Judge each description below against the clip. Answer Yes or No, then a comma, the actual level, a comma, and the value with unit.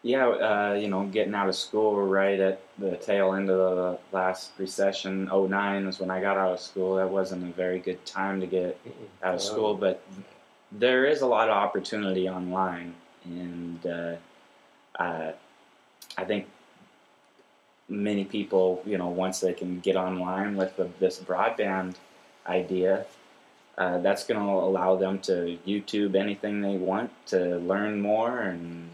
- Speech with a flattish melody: Yes, narrow, 1.3 semitones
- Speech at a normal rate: Yes, average, 165 wpm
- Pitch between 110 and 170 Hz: No, very low, 95 Hz